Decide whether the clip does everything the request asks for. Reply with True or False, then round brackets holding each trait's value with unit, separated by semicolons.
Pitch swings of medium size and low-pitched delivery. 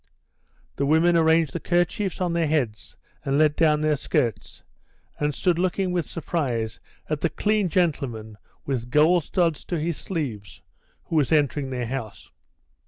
False (4.2 semitones; 155 Hz)